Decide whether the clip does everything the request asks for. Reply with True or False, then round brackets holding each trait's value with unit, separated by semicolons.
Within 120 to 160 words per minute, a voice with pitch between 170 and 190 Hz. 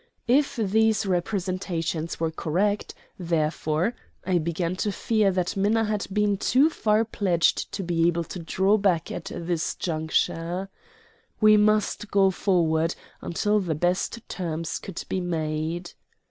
True (135 wpm; 185 Hz)